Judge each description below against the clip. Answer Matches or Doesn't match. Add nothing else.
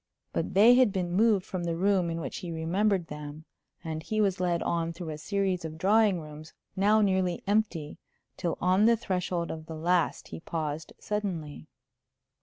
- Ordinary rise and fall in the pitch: Matches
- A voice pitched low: Doesn't match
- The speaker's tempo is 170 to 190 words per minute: Matches